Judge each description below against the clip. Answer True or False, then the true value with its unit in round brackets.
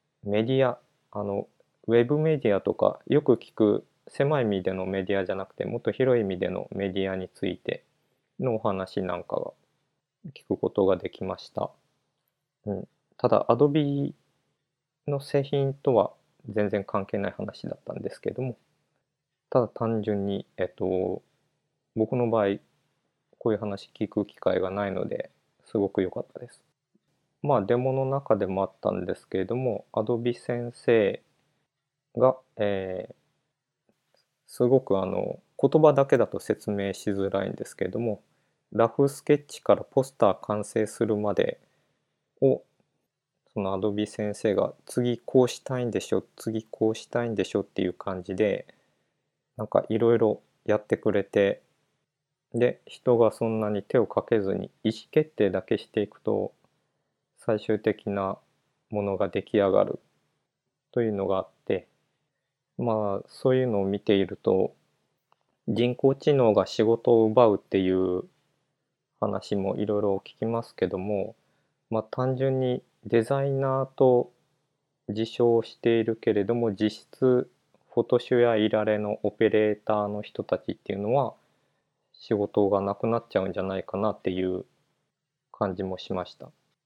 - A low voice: True (110 Hz)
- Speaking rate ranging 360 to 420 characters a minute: False (285 characters per minute)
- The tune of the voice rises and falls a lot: False (4.0 semitones)